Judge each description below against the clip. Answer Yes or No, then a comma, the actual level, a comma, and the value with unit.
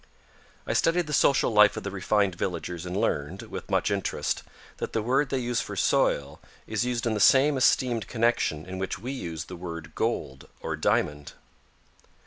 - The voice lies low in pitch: Yes, low, 105 Hz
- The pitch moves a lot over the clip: Yes, wide, 5.9 semitones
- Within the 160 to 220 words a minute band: Yes, average, 180 wpm